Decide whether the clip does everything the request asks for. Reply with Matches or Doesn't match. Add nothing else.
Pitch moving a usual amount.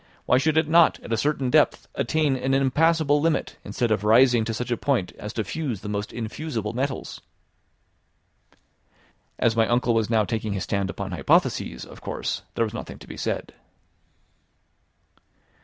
Matches